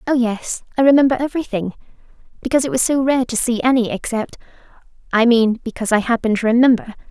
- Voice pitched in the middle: No, high, 240 Hz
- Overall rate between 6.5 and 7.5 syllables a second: Yes, 6.9 syllables/s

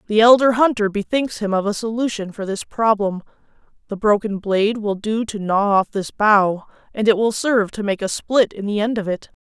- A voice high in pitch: Yes, high, 210 Hz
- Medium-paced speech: No, fast, 215 wpm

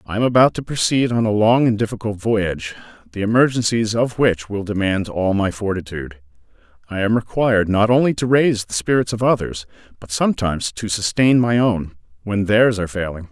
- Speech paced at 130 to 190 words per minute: Yes, average, 185 wpm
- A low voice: Yes, low, 105 Hz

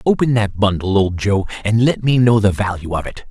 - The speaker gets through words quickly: Yes, fast, 235 wpm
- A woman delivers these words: No, male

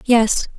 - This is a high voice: Yes, high, 230 Hz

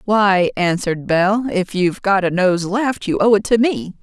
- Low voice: No, high, 190 Hz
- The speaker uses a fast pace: Yes, fast, 210 wpm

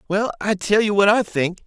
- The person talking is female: No, male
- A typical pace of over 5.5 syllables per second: No, 5.3 syllables/s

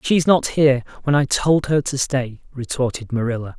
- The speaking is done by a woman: No, male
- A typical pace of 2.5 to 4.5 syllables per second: No, 5.1 syllables/s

